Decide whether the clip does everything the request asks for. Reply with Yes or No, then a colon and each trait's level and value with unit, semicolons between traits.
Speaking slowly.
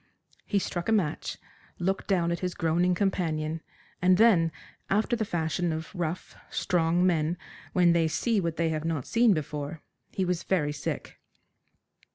No: average, 160 wpm